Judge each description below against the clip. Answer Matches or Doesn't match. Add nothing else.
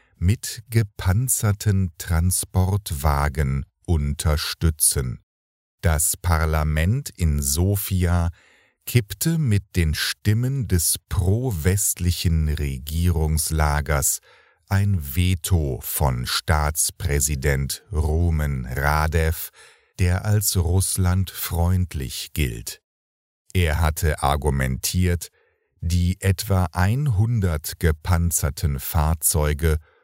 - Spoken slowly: Matches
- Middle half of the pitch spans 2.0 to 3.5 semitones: Doesn't match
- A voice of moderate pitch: Doesn't match